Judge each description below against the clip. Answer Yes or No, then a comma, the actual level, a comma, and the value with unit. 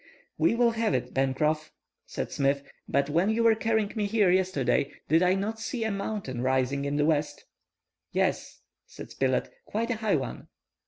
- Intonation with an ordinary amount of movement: No, wide, 7.9 semitones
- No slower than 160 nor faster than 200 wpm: Yes, average, 170 wpm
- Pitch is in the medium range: Yes, medium, 175 Hz